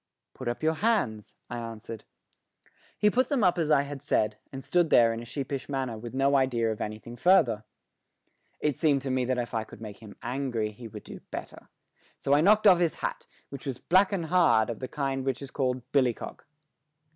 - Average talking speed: No, fast, 215 wpm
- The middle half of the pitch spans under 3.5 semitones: No, average, 4.7 semitones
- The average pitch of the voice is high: No, low, 130 Hz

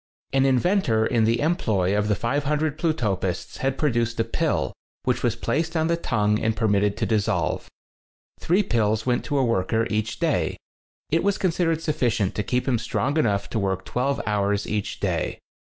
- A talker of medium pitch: No, low, 115 Hz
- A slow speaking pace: No, average, 185 wpm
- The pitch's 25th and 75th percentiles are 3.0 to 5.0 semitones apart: No, wide, 5.6 semitones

